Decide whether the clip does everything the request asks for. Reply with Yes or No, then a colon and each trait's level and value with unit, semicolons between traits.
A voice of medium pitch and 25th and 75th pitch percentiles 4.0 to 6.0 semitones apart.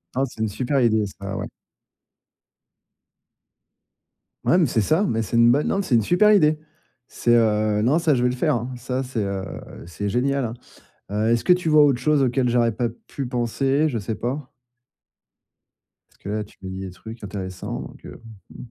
No: low, 120 Hz; average, 4.3 semitones